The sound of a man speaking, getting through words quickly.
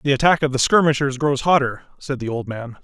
Yes: male; fast, 235 wpm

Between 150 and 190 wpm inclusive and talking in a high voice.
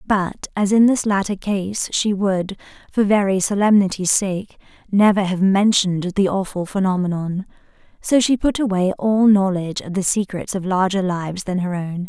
Yes: average, 165 wpm; high, 195 Hz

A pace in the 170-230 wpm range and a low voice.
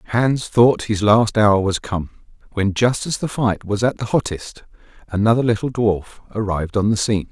Yes: average, 190 wpm; low, 110 Hz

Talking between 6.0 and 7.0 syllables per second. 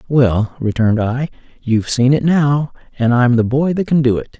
No: 5.0 syllables/s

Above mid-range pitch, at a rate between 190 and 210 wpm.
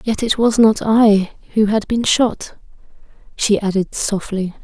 No: high, 210 Hz; average, 155 wpm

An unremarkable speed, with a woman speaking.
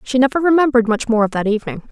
No: fast, 250 wpm; female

